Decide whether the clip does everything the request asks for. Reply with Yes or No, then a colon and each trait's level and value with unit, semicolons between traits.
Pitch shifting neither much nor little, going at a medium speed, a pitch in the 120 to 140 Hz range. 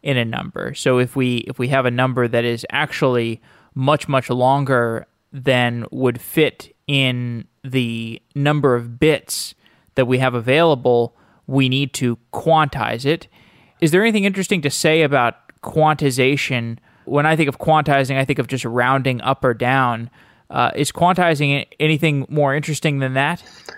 Yes: average, 3.1 semitones; average, 160 wpm; low, 135 Hz